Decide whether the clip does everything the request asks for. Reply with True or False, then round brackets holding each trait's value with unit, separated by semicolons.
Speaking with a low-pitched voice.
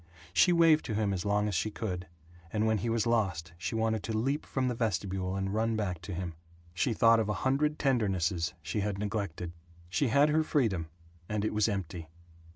True (105 Hz)